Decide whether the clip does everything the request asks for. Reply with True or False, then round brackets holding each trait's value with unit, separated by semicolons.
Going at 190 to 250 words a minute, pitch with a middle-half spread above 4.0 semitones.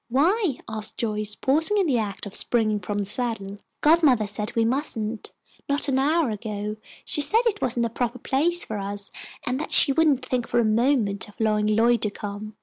True (200 wpm; 4.7 semitones)